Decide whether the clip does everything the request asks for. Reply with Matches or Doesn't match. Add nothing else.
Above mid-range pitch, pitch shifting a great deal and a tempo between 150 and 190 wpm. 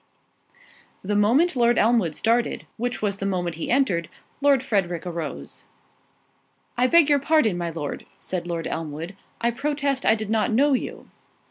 Matches